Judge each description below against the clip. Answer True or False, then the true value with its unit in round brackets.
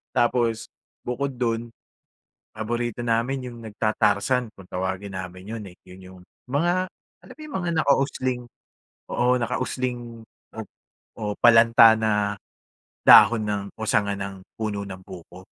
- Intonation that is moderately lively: True (3.4 semitones)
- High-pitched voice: False (115 Hz)